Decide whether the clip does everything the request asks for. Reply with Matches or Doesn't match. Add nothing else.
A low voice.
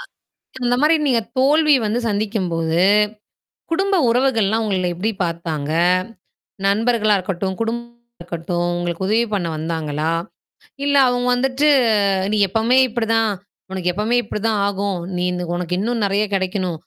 Doesn't match